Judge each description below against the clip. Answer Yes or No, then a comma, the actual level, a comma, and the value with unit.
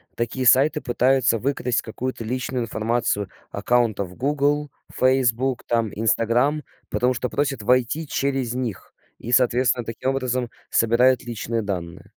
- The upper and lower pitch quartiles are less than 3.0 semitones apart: Yes, narrow, 2.4 semitones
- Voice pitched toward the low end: Yes, low, 125 Hz